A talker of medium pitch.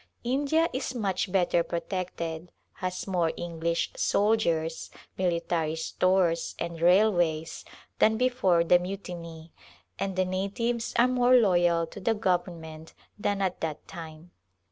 Yes: medium, 180 Hz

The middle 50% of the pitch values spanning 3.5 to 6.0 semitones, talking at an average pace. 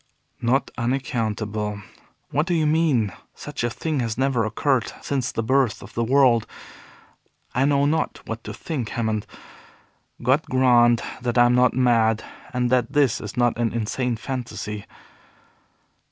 No: average, 3.1 semitones; average, 150 wpm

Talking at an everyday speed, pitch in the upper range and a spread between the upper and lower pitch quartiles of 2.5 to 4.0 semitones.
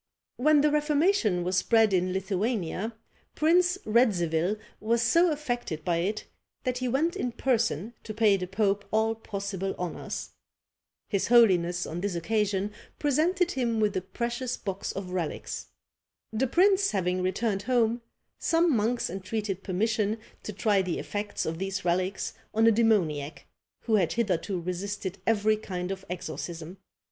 No: average, 145 wpm; high, 210 Hz; average, 4.4 semitones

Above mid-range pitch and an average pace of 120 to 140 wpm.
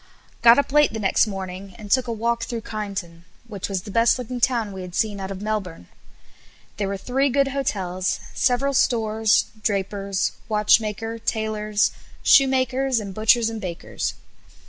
No: high, 215 Hz; average, 160 wpm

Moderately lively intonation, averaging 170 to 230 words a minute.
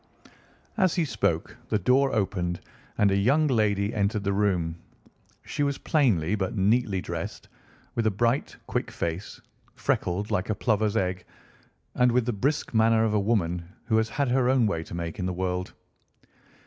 Yes: average, 4.6 semitones; average, 175 wpm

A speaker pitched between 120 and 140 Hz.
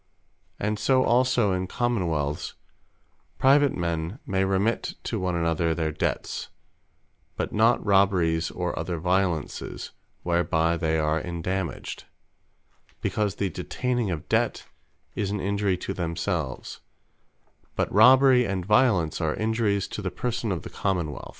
No: very low, 95 Hz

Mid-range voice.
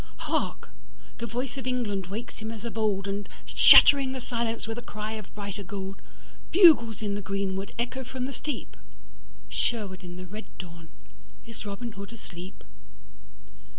No: high, 215 Hz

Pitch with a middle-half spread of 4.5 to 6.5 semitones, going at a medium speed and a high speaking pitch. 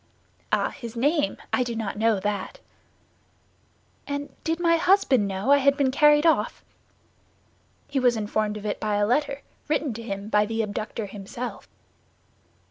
Yes: wide, 5.4 semitones; average, 155 wpm; high, 235 Hz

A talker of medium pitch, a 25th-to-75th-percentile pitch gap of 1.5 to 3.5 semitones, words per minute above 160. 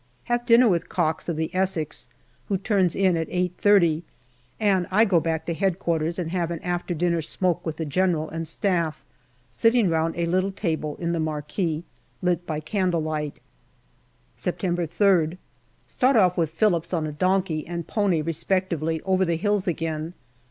Yes: medium, 170 Hz; average, 2.7 semitones; average, 170 wpm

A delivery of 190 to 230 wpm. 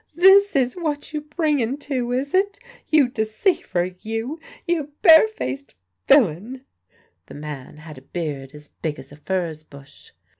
No: average, 155 wpm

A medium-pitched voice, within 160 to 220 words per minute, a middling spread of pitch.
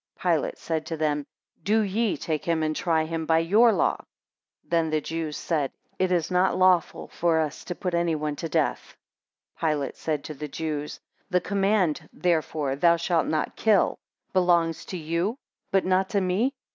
Yes: medium, 165 Hz; average, 185 wpm; average, 3.1 semitones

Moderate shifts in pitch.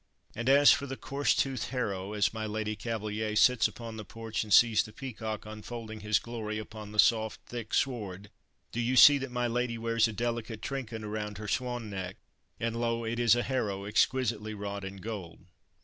No: narrow, 2.2 semitones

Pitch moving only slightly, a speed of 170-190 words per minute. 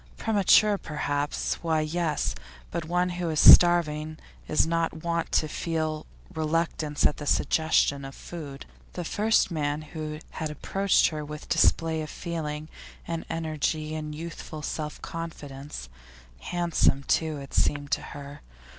No: narrow, 1.9 semitones; slow, 135 wpm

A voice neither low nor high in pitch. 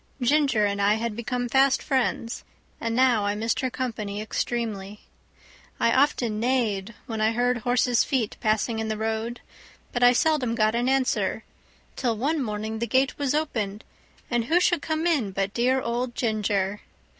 No: high, 235 Hz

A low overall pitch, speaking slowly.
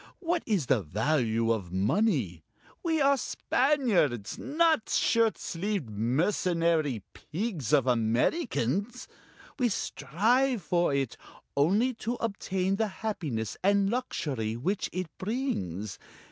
No: medium, 180 Hz; slow, 110 wpm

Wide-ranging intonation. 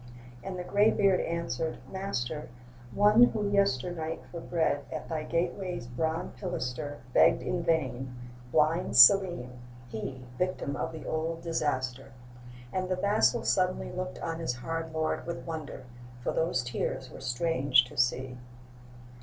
Yes: wide, 5.7 semitones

